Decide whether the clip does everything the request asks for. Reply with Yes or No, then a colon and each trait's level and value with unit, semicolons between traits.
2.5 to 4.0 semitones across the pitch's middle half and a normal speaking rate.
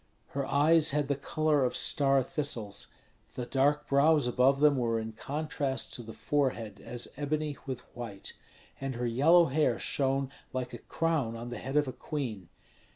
Yes: average, 3.3 semitones; average, 170 wpm